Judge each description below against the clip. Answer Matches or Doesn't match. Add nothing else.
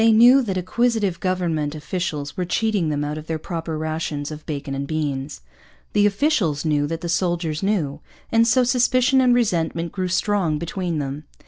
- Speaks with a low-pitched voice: Doesn't match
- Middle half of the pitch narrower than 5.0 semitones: Doesn't match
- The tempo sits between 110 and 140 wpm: Doesn't match